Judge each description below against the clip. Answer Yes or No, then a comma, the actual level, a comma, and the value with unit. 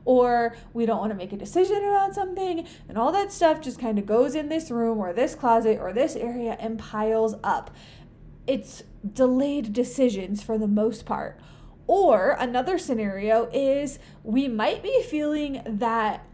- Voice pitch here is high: Yes, high, 245 Hz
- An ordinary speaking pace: Yes, average, 165 wpm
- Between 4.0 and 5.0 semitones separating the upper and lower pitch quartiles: Yes, average, 4.7 semitones